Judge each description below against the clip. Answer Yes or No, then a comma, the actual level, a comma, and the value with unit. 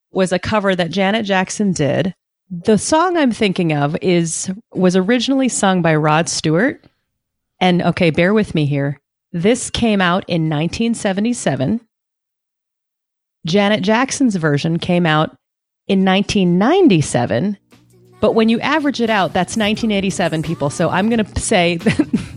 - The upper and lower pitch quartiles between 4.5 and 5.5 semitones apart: Yes, average, 4.9 semitones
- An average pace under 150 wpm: Yes, average, 140 wpm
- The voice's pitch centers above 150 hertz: Yes, medium, 185 Hz